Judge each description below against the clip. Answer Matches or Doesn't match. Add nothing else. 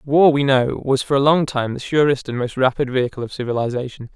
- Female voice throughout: Doesn't match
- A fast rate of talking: Matches